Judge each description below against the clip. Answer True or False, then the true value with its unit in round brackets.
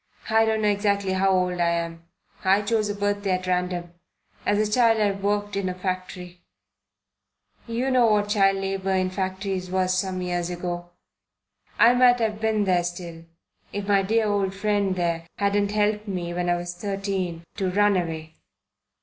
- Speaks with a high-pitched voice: True (195 Hz)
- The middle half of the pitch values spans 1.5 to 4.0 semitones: True (2.4 semitones)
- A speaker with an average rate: True (175 wpm)